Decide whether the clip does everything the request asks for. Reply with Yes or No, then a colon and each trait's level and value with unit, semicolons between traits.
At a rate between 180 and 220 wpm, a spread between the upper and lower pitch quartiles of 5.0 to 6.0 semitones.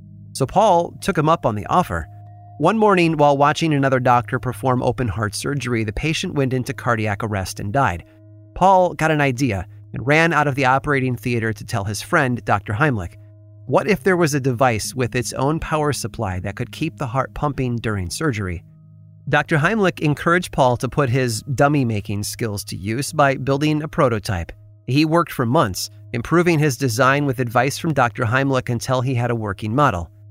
Yes: average, 190 wpm; wide, 5.5 semitones